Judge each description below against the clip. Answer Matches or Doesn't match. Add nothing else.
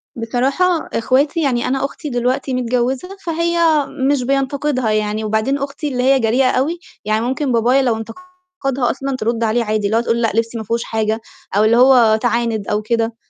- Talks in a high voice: Matches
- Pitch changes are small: Doesn't match